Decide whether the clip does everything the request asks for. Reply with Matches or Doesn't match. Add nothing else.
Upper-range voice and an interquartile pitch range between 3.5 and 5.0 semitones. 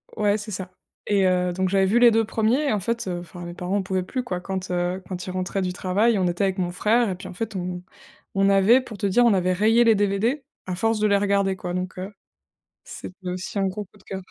Doesn't match